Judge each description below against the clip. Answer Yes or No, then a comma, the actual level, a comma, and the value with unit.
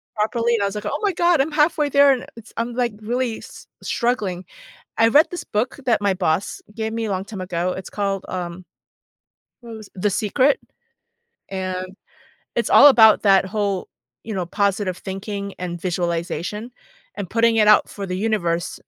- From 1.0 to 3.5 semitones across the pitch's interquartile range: No, average, 3.9 semitones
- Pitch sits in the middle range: No, high, 210 Hz